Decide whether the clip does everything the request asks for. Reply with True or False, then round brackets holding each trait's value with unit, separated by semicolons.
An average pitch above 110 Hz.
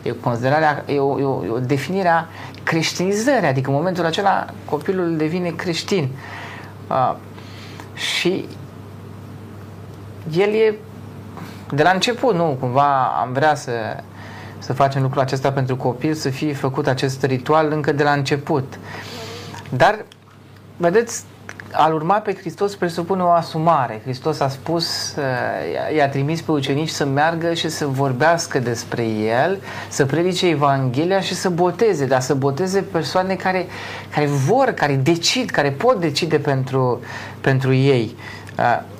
True (140 Hz)